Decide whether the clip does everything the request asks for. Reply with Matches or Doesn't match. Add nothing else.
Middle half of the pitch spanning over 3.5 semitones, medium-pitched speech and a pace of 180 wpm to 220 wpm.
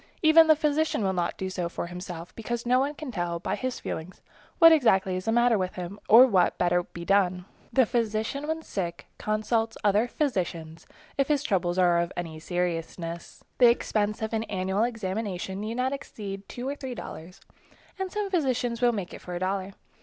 Doesn't match